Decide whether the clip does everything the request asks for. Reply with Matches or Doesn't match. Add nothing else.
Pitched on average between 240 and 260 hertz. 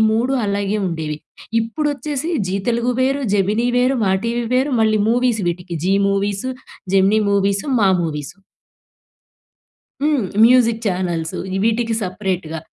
Doesn't match